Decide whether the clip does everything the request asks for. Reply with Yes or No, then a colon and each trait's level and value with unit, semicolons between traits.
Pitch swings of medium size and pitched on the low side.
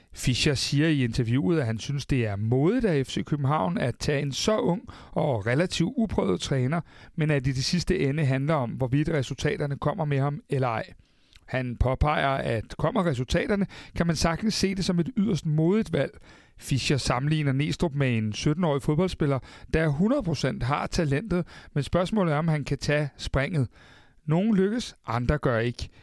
No: average, 4.3 semitones; medium, 150 Hz